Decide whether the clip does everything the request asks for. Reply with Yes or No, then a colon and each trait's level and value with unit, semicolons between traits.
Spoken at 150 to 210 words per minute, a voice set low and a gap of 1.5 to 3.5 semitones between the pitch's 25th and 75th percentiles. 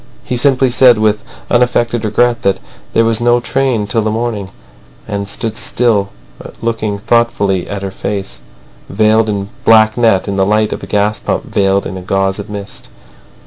Yes: average, 170 wpm; low, 110 Hz; average, 2.7 semitones